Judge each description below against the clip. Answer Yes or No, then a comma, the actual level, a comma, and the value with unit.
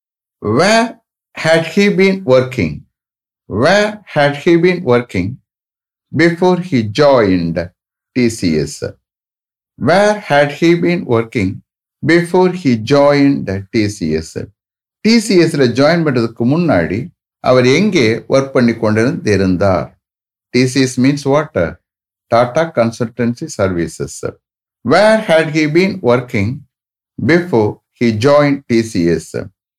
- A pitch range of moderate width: No, wide, 6.6 semitones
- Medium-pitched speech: No, low, 130 Hz